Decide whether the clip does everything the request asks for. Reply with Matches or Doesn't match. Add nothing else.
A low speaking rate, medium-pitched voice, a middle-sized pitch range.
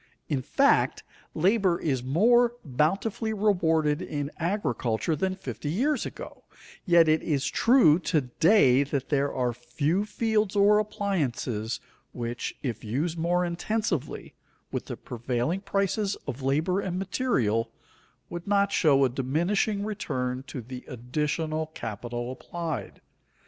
Doesn't match